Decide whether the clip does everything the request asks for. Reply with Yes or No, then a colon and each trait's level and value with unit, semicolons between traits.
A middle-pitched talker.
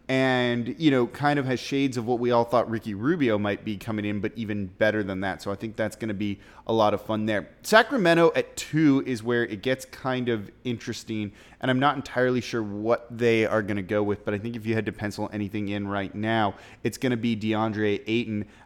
No: low, 115 Hz